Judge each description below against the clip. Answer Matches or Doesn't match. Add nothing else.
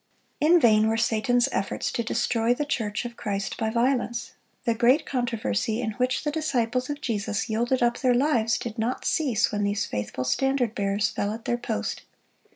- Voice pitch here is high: Matches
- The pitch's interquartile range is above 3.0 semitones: Doesn't match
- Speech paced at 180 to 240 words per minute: Matches